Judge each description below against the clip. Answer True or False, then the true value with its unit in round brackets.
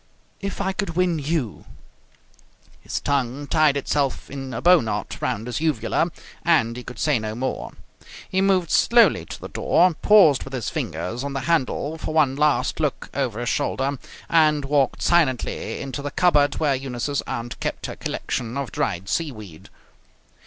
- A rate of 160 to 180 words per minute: True (170 wpm)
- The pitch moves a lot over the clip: False (4.4 semitones)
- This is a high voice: False (140 Hz)